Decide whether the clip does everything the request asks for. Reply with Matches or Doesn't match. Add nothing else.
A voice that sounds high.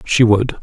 Doesn't match